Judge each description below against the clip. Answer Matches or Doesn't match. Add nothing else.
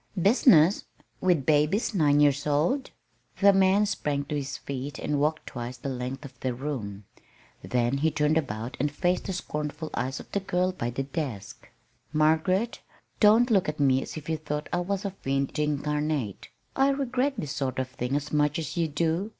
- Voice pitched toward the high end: Doesn't match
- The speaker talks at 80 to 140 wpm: Doesn't match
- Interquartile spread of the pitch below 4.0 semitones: Doesn't match